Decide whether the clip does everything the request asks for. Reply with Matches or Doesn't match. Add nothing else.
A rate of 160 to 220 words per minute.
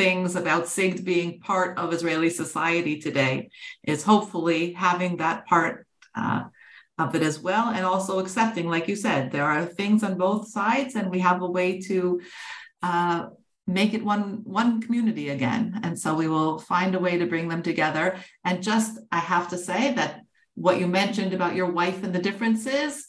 Matches